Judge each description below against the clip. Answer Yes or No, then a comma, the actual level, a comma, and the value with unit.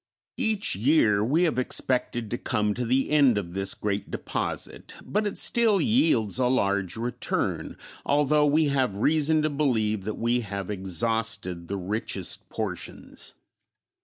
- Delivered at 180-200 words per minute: No, average, 145 wpm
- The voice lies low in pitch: Yes, low, 120 Hz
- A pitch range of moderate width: No, wide, 6.4 semitones